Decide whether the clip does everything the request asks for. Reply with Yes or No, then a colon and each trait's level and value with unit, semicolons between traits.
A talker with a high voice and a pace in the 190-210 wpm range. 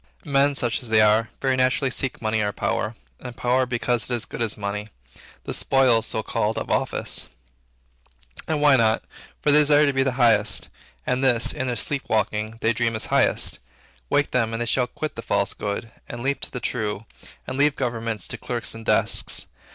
No: low, 120 Hz; average, 200 wpm